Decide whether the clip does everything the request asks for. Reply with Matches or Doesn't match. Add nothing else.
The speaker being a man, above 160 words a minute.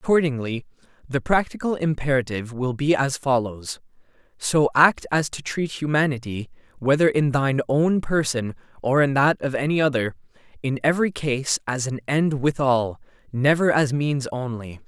Doesn't match